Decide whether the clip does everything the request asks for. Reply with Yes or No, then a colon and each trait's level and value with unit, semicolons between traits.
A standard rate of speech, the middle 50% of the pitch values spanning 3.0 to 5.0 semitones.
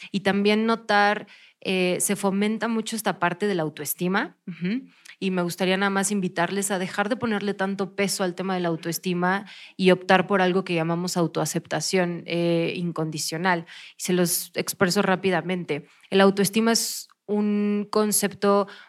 No: average, 155 wpm; narrow, 2.5 semitones